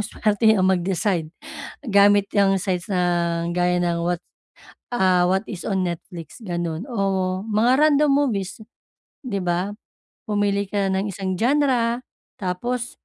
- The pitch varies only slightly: No, average, 3.7 semitones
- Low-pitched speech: No, high, 195 Hz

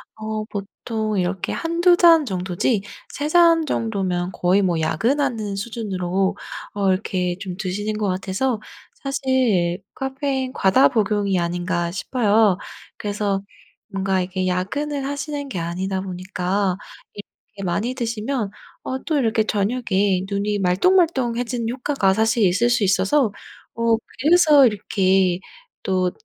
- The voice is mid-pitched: No, high, 205 Hz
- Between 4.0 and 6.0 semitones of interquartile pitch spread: Yes, average, 5.2 semitones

